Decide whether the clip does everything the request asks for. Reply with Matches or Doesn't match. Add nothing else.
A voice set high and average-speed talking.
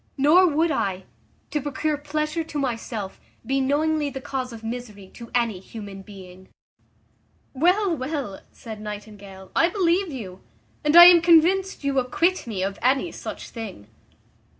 Matches